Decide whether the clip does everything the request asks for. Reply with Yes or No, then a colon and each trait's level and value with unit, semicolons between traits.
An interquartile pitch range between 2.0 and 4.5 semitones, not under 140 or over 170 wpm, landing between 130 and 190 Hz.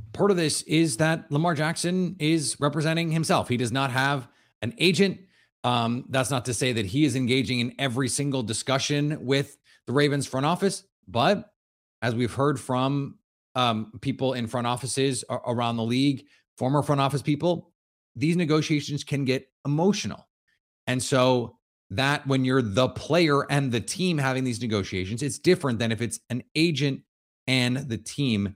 Yes: average, 3.4 semitones; average, 165 wpm; low, 135 Hz